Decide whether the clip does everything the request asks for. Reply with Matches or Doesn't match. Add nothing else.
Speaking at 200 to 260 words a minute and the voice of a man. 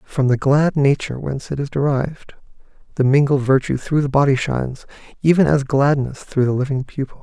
Doesn't match